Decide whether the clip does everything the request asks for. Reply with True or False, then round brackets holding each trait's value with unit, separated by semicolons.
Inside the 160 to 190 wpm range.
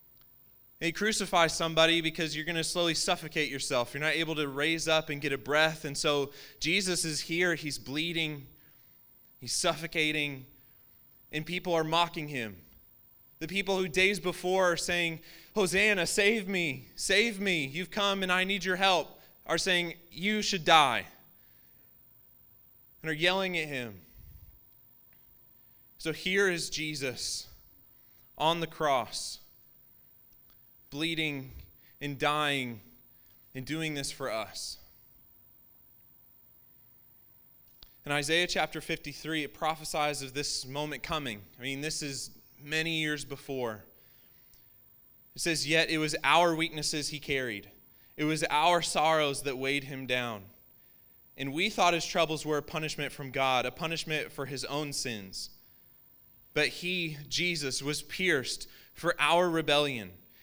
False (135 wpm)